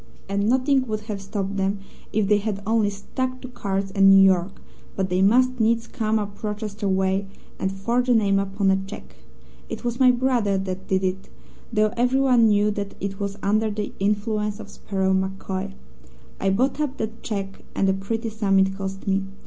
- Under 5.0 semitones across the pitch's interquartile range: Yes, narrow, 2.5 semitones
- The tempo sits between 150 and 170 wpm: No, average, 190 wpm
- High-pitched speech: Yes, high, 205 Hz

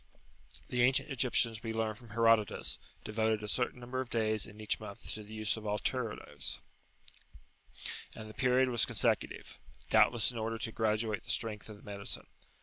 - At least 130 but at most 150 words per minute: No, average, 170 wpm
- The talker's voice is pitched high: No, low, 110 Hz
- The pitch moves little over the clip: Yes, narrow, 2.0 semitones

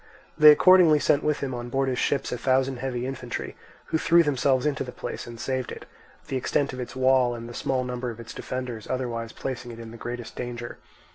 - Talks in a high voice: No, low, 130 Hz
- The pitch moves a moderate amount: No, narrow, 1.9 semitones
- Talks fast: Yes, fast, 220 wpm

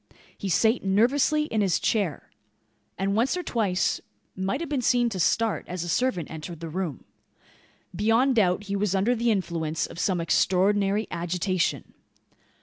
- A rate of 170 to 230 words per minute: No, average, 155 wpm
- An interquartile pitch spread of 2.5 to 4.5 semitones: Yes, average, 4.1 semitones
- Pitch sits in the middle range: No, high, 195 Hz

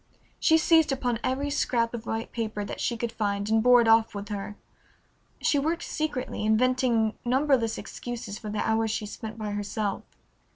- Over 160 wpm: Yes, average, 175 wpm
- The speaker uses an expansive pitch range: No, average, 2.9 semitones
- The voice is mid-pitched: No, high, 230 Hz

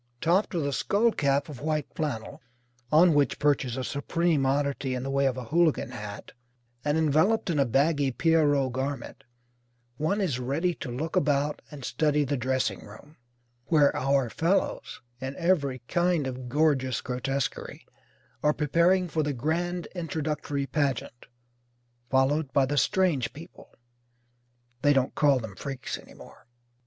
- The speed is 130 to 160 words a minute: Yes, average, 150 wpm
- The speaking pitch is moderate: Yes, medium, 145 Hz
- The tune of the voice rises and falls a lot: No, average, 3.3 semitones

